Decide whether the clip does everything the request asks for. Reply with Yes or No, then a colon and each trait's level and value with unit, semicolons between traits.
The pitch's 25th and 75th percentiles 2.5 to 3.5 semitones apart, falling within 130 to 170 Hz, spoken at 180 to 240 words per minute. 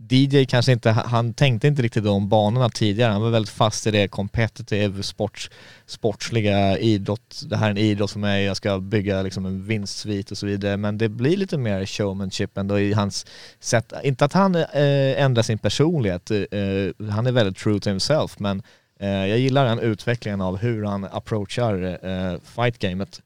No: average, 3.2 semitones; low, 105 Hz; average, 190 wpm